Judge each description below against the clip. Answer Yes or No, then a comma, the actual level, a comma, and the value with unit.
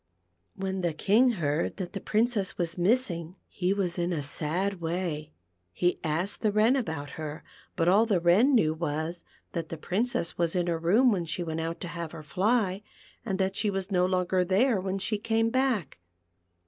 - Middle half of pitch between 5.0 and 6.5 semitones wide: No, average, 3.7 semitones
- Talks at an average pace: Yes, average, 190 wpm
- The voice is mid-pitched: Yes, medium, 180 Hz